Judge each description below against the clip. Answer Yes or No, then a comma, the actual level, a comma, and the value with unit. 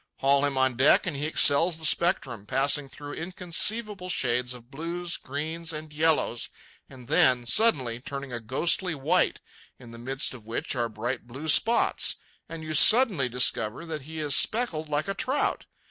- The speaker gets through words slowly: No, average, 170 wpm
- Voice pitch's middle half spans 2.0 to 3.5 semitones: No, average, 4.7 semitones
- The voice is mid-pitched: Yes, medium, 145 Hz